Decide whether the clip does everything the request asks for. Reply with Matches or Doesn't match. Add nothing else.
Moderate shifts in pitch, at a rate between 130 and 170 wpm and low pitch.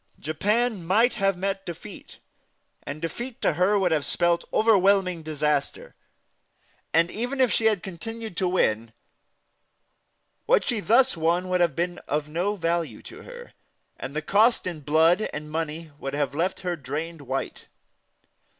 Doesn't match